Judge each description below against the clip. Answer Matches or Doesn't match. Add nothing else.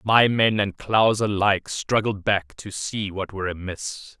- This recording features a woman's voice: Doesn't match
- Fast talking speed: Doesn't match